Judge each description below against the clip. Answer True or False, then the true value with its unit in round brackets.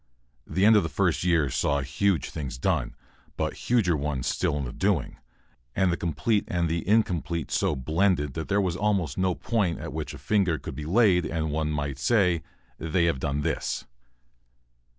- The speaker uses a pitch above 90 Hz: False (85 Hz)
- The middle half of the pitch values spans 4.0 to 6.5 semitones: True (4.6 semitones)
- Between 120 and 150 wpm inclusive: False (185 wpm)